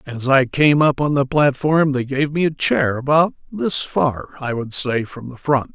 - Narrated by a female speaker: No, male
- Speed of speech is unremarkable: No, fast, 220 wpm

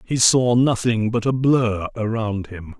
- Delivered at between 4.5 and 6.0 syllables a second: No, 4.0 syllables/s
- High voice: No, low, 115 Hz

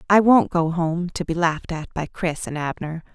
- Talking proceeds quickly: Yes, fast, 230 wpm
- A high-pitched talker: No, medium, 170 Hz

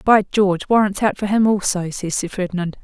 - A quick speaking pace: Yes, fast, 210 wpm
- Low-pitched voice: No, high, 195 Hz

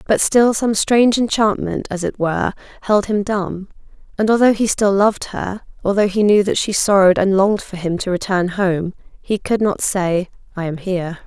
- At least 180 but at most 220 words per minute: Yes, average, 195 wpm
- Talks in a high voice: Yes, high, 200 Hz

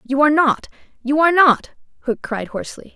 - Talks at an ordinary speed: Yes, average, 185 wpm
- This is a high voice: Yes, very high, 275 Hz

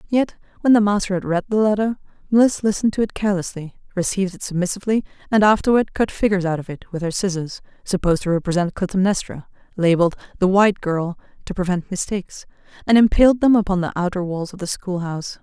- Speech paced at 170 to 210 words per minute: Yes, average, 185 wpm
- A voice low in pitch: No, high, 190 Hz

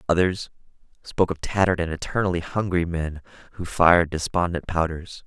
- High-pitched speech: No, very low, 85 Hz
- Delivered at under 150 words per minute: Yes, slow, 135 wpm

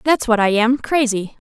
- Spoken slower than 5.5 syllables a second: Yes, 4.7 syllables/s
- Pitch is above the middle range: Yes, high, 235 Hz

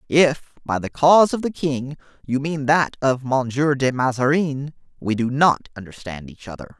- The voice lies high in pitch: No, low, 135 Hz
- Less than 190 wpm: Yes, average, 175 wpm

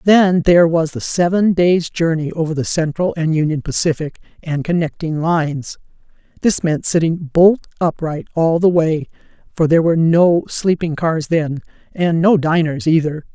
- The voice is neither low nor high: Yes, medium, 165 Hz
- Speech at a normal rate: Yes, average, 155 wpm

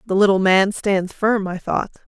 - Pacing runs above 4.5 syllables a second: No, 4.4 syllables/s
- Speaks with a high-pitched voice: Yes, high, 195 Hz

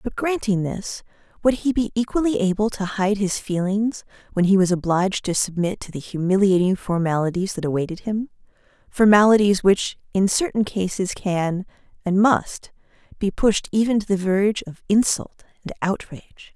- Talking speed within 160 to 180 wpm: No, average, 150 wpm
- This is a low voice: No, high, 200 Hz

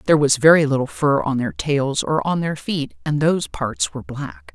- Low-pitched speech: Yes, low, 130 Hz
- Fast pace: Yes, fast, 225 wpm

